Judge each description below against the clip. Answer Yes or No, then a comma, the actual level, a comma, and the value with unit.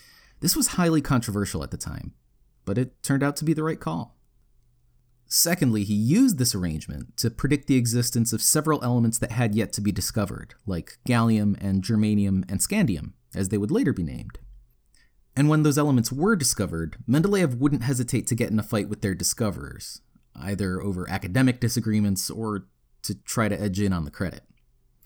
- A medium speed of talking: Yes, average, 180 wpm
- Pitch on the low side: Yes, low, 115 Hz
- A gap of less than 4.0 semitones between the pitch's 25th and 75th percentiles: No, average, 4.8 semitones